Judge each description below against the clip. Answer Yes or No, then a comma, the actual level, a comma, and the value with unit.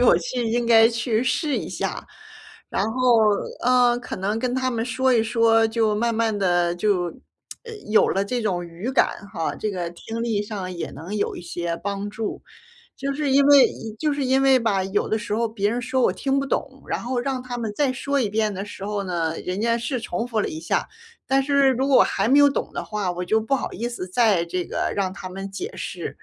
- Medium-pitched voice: No, high, 225 Hz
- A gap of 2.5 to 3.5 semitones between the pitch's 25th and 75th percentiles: No, average, 4.3 semitones